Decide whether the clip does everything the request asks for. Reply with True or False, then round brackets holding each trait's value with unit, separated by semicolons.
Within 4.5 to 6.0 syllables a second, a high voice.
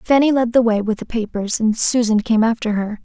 True (5.5 syllables/s; 225 Hz)